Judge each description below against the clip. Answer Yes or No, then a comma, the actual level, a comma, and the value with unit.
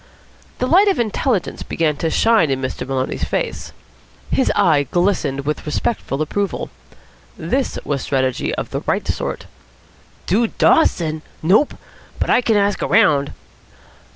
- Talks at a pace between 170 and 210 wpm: No, slow, 135 wpm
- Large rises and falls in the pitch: Yes, wide, 8.0 semitones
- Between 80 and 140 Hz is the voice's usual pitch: No, medium, 175 Hz